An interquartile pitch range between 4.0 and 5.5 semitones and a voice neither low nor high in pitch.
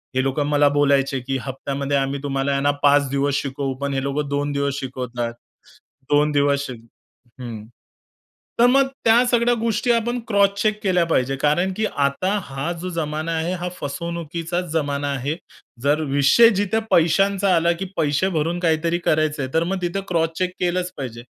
Yes: average, 4.4 semitones; medium, 150 Hz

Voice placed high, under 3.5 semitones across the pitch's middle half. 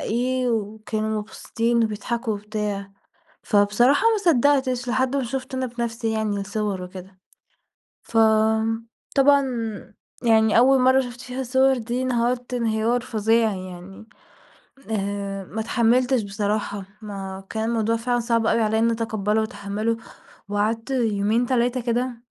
Yes: high, 225 Hz; average, 2.7 semitones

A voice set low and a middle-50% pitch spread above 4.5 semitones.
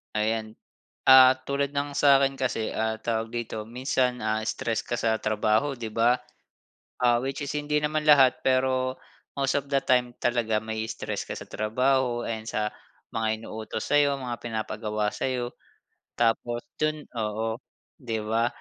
No: low, 120 Hz; average, 3.3 semitones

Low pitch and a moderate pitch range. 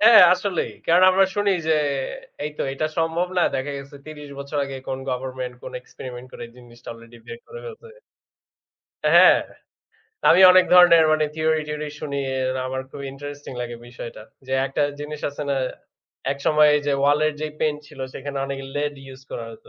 No: medium, 145 Hz; average, 3.4 semitones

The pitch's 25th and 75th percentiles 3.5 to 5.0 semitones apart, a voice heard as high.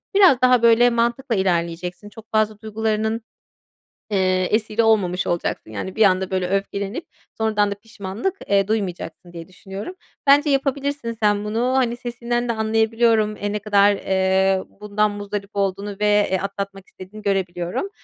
No: average, 3.0 semitones; high, 210 Hz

